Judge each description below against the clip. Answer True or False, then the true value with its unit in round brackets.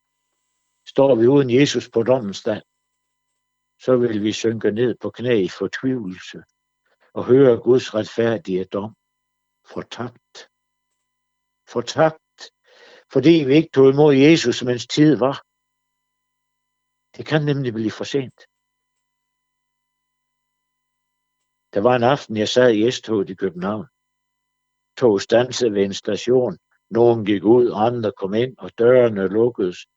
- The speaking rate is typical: False (130 wpm)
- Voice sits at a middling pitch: True (145 Hz)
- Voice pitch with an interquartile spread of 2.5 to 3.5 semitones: True (3.0 semitones)